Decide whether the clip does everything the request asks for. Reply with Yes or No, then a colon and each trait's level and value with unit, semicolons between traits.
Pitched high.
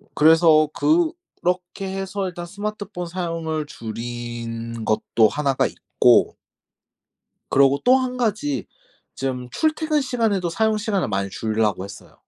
No: medium, 170 Hz